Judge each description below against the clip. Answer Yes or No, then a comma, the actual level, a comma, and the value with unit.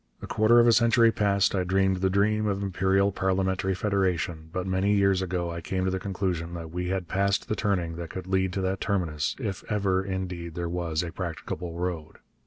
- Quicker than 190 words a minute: Yes, fast, 205 wpm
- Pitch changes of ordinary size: No, narrow, 2.0 semitones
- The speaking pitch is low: Yes, very low, 95 Hz